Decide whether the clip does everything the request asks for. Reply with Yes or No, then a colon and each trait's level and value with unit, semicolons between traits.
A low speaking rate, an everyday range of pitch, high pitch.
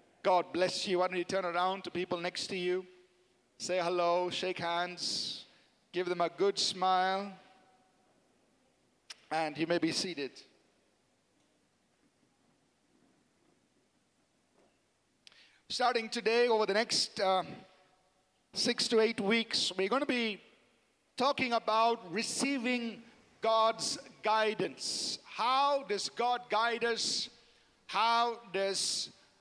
Yes: slow, 110 wpm; average, 4.2 semitones; high, 195 Hz